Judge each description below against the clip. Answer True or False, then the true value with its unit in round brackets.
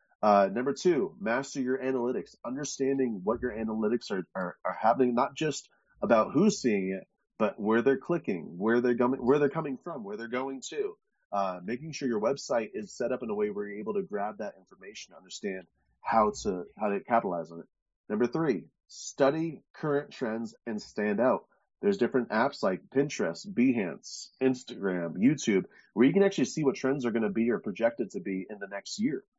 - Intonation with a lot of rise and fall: True (6.2 semitones)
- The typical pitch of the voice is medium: False (130 Hz)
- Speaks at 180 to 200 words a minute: True (195 wpm)